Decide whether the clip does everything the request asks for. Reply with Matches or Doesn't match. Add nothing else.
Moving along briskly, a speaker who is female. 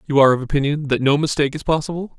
Doesn't match